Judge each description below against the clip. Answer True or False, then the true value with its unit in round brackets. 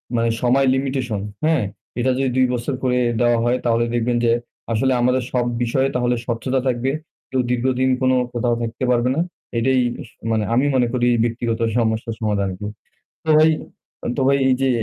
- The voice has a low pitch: True (125 Hz)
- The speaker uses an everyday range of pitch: False (2.0 semitones)